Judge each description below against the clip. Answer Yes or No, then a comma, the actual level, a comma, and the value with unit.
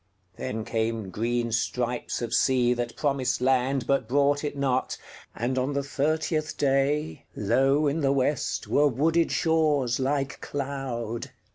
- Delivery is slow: Yes, slow, 130 wpm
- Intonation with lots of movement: No, average, 3.0 semitones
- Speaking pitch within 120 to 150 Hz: Yes, low, 135 Hz